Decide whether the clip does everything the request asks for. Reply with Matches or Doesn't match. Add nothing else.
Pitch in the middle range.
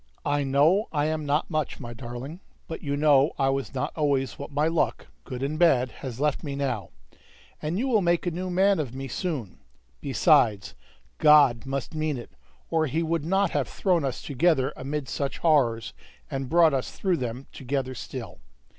Matches